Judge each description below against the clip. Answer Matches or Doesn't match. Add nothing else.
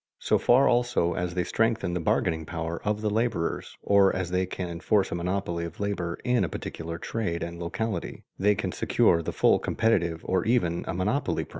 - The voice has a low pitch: Matches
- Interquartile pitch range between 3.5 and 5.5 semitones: Matches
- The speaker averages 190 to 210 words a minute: Matches